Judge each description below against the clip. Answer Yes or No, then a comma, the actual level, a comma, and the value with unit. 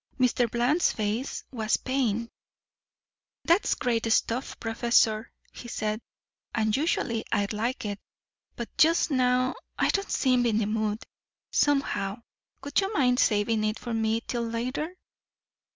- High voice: Yes, high, 235 Hz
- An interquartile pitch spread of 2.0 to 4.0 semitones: Yes, average, 2.8 semitones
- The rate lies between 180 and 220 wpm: No, slow, 135 wpm